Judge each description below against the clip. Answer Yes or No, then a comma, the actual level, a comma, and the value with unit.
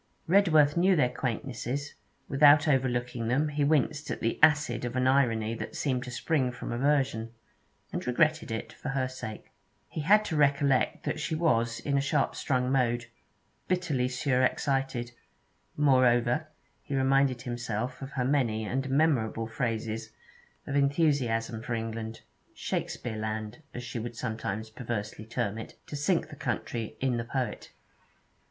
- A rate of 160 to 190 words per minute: No, average, 145 wpm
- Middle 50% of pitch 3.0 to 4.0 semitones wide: Yes, average, 3.6 semitones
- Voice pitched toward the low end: Yes, low, 130 Hz